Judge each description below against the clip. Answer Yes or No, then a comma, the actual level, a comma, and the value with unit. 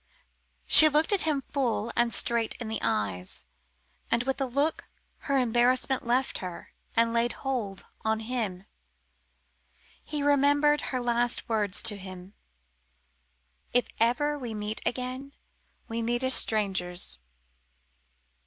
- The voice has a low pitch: No, high, 240 Hz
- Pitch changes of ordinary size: Yes, average, 3.7 semitones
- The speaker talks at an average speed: No, slow, 125 wpm